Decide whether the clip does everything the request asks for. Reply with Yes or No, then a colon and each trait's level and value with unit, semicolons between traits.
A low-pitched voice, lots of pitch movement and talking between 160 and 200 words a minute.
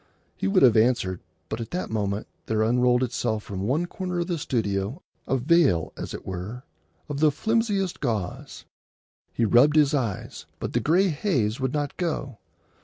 Yes: low, 125 Hz; wide, 6.3 semitones; average, 175 wpm